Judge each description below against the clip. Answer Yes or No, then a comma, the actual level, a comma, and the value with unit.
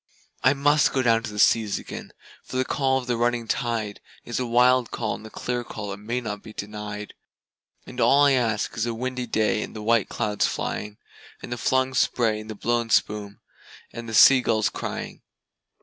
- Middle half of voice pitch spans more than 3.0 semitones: No, average, 2.7 semitones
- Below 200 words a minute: No, fast, 205 wpm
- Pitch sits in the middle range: No, low, 115 Hz